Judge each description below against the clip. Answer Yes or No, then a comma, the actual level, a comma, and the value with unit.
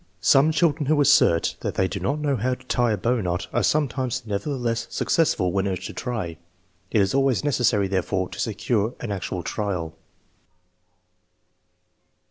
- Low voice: Yes, low, 115 Hz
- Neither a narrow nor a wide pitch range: No, wide, 5.9 semitones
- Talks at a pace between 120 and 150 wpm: No, average, 160 wpm